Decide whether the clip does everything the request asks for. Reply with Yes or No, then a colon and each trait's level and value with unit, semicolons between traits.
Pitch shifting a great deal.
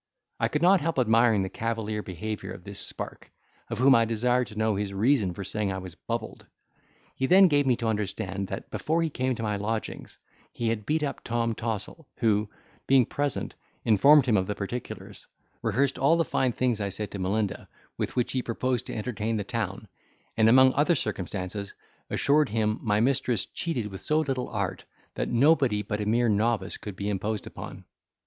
No: average, 3.9 semitones